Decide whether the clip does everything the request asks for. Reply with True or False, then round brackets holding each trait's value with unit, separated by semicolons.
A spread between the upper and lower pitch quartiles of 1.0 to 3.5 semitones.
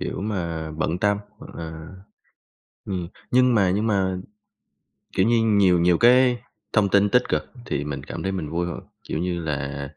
False (4.3 semitones)